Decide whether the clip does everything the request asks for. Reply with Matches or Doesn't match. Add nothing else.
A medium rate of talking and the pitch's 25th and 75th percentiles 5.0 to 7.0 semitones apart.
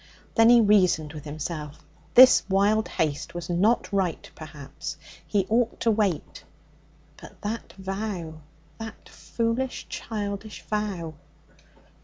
Doesn't match